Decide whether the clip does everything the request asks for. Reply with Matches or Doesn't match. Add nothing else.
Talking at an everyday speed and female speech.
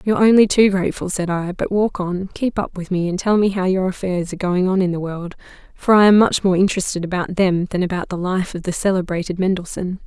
Doesn't match